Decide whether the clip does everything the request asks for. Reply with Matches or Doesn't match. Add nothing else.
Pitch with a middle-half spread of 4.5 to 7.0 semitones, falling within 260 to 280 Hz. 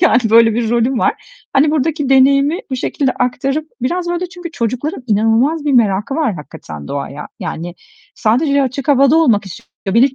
Matches